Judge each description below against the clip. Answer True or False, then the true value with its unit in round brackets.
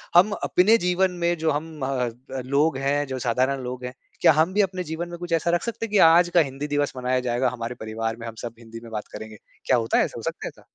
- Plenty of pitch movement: True (5.7 semitones)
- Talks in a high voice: False (140 Hz)